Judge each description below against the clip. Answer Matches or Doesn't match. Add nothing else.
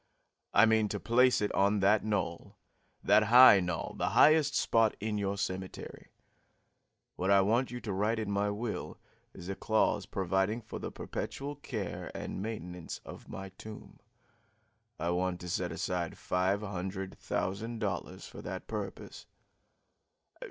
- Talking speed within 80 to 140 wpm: Doesn't match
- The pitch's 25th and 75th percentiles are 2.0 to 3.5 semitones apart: Matches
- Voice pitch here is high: Doesn't match